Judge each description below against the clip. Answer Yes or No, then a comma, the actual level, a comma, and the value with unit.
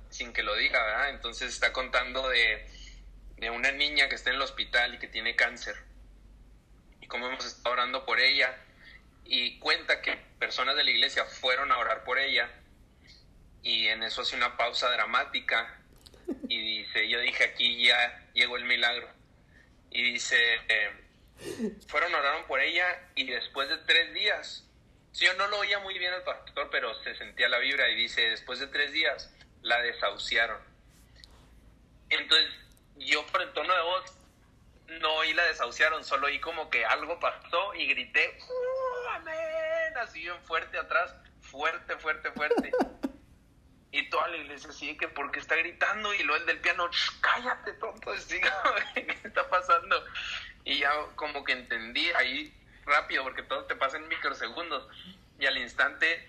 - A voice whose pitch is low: No, medium, 175 Hz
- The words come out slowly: No, average, 165 wpm